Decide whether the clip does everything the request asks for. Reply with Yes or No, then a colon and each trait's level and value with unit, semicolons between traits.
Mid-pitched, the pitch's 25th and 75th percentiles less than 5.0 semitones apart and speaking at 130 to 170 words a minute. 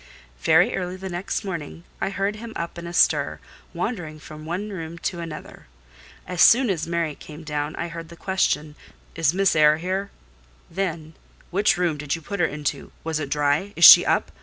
No: medium, 170 Hz; average, 3.5 semitones; average, 185 wpm